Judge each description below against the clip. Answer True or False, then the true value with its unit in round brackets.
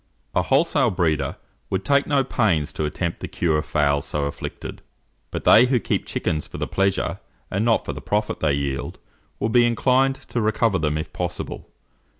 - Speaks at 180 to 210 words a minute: True (185 wpm)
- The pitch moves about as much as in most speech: False (7.8 semitones)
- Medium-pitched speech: False (95 Hz)